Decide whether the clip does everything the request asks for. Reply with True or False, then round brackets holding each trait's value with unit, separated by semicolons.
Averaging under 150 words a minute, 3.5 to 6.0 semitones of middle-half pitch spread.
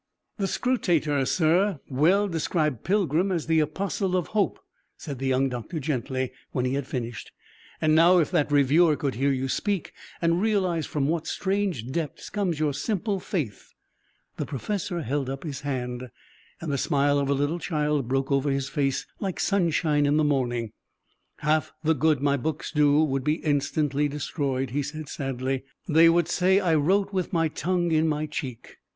False (180 wpm; 3.9 semitones)